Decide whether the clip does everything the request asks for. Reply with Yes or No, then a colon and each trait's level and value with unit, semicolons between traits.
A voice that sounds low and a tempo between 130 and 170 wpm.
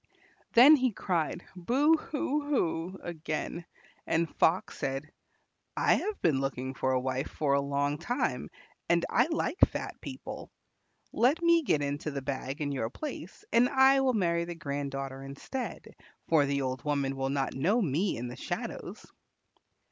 No: medium, 155 Hz; average, 165 wpm